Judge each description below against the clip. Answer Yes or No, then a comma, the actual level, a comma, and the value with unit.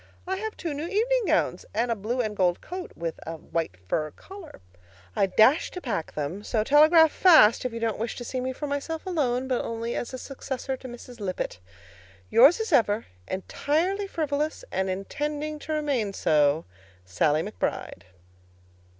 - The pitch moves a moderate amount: No, wide, 7.1 semitones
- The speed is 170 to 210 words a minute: Yes, average, 175 wpm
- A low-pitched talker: No, very high, 255 Hz